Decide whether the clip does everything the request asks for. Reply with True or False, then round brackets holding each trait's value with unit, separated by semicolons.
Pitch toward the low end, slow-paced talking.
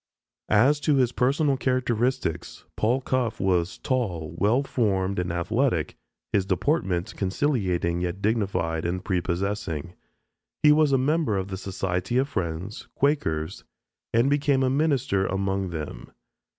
True (100 Hz; 130 wpm)